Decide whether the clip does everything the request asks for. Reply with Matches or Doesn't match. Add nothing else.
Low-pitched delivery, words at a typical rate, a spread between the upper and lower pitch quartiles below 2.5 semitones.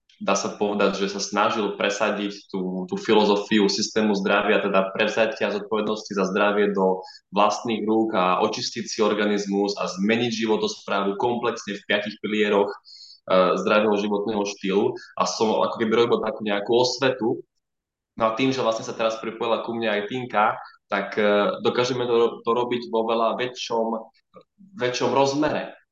Matches